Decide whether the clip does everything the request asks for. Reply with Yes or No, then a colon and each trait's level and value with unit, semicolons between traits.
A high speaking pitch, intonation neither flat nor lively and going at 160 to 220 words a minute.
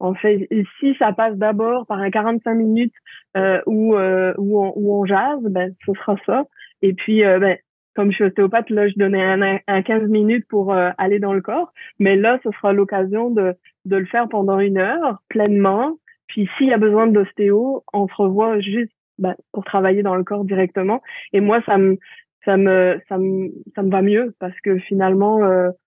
No: high, 200 Hz; narrow, 2.2 semitones; average, 210 wpm